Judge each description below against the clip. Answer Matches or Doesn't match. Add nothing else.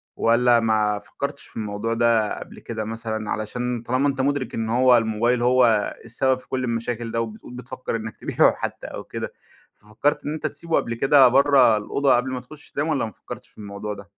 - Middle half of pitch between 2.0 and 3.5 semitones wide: Matches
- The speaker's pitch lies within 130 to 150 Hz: Doesn't match